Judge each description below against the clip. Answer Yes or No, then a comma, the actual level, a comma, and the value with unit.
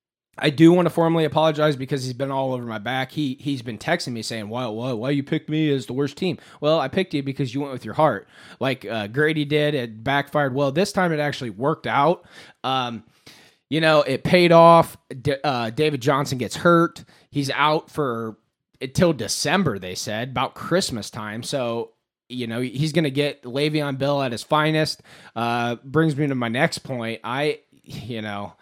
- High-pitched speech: No, medium, 140 Hz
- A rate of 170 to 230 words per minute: Yes, fast, 205 wpm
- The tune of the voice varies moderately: Yes, average, 4.1 semitones